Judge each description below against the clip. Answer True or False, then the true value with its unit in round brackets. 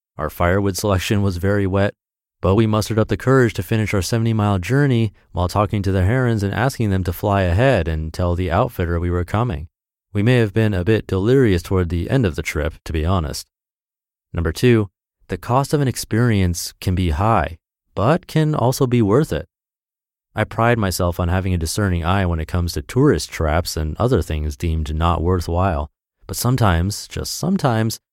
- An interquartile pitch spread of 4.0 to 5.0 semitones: True (4.4 semitones)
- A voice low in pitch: True (100 Hz)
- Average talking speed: True (195 wpm)